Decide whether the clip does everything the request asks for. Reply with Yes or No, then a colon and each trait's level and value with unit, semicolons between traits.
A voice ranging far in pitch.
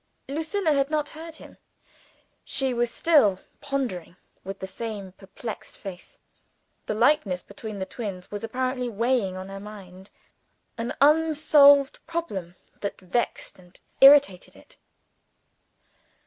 Yes: wide, 6.7 semitones